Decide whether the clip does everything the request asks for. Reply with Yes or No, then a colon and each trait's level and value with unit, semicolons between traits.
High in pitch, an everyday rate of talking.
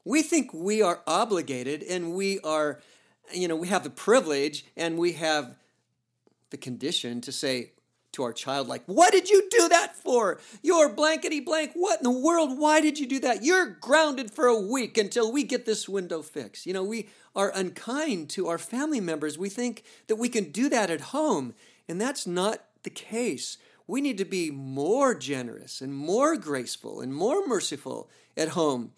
Yes: high, 215 Hz; average, 190 wpm